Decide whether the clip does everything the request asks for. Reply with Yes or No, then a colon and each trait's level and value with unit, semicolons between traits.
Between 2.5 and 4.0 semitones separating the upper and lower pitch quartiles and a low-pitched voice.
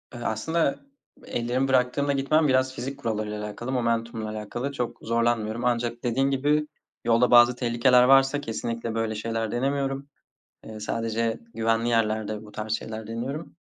Yes: average, 2.8 semitones; low, 120 Hz